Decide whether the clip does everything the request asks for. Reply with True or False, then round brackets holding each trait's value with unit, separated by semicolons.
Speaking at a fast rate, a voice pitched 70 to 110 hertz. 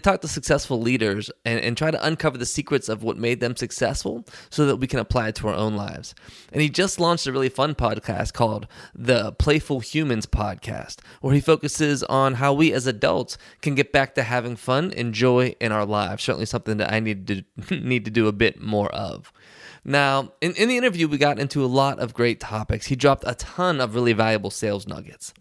False (220 wpm; 125 Hz)